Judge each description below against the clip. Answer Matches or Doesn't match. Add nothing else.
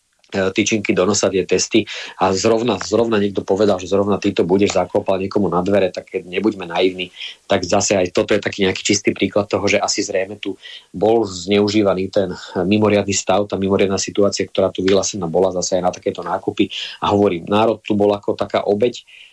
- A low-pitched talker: Matches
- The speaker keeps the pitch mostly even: Matches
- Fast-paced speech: Matches